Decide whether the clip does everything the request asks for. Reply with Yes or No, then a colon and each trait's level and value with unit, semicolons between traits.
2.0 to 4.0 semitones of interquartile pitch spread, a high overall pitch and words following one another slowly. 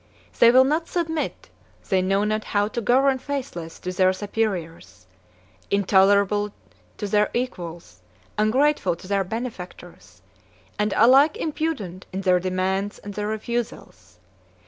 No: average, 4.6 semitones; high, 205 Hz; slow, 125 wpm